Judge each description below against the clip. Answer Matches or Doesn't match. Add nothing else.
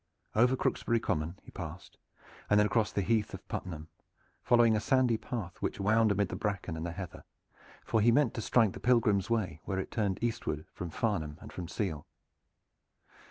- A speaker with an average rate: Matches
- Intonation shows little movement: Doesn't match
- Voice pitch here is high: Doesn't match